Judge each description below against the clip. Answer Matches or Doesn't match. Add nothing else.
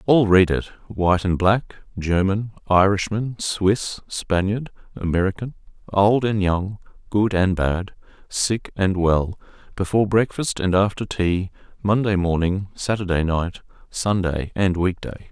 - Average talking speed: Doesn't match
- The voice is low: Matches